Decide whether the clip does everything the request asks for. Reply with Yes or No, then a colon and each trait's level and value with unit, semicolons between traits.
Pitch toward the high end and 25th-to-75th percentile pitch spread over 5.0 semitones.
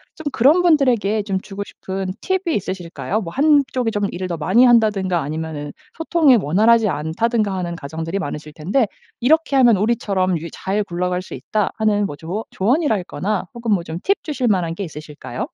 Yes: high, 200 Hz; wide, 5.4 semitones